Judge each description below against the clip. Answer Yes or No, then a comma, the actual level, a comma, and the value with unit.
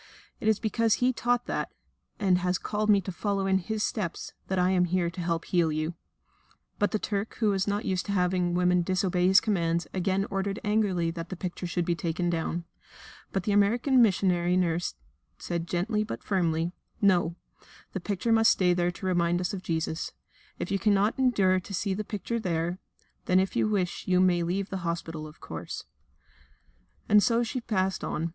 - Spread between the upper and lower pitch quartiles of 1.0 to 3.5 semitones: Yes, average, 2.8 semitones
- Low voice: No, medium, 185 Hz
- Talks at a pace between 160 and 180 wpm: No, average, 195 wpm